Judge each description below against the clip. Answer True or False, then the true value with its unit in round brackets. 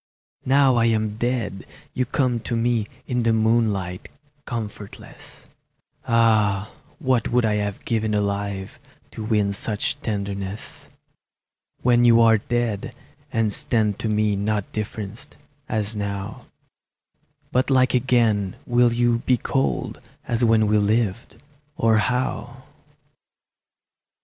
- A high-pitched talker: False (110 Hz)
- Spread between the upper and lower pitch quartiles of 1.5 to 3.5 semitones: True (2.6 semitones)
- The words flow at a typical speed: False (120 wpm)